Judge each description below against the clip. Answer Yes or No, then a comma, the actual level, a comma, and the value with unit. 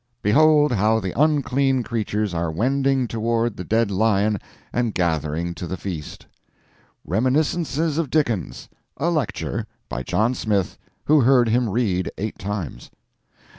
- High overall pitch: No, low, 115 Hz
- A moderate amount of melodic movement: No, wide, 5.7 semitones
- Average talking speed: No, slow, 130 wpm